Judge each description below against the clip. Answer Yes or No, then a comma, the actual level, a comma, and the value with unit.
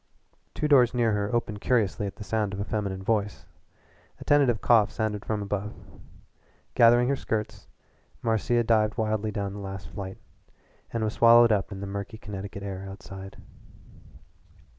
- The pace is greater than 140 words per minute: Yes, average, 160 wpm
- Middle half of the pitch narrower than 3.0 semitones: Yes, narrow, 2.5 semitones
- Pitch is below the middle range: Yes, low, 105 Hz